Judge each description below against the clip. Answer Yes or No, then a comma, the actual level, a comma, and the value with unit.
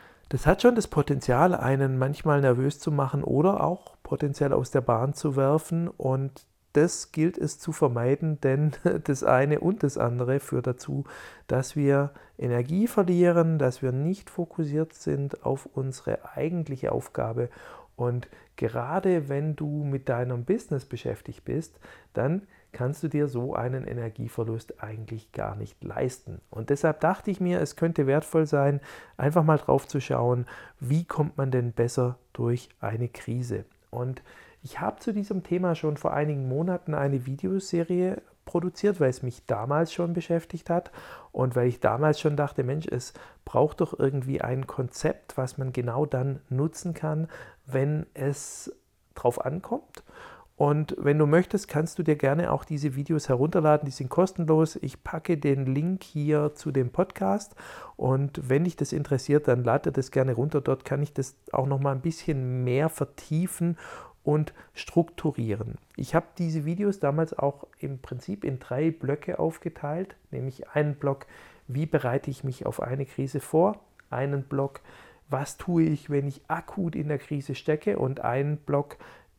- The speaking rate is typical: Yes, average, 160 wpm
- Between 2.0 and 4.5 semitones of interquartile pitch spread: Yes, average, 3.6 semitones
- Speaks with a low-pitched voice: No, medium, 145 Hz